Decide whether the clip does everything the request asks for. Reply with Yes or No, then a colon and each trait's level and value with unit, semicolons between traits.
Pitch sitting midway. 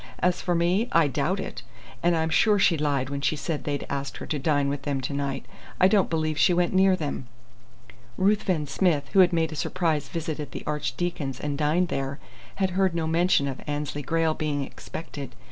Yes: medium, 155 Hz